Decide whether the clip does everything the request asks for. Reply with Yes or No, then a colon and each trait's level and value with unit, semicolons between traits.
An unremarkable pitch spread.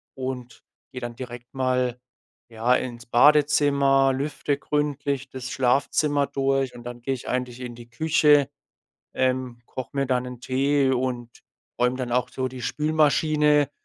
No: narrow, 2.3 semitones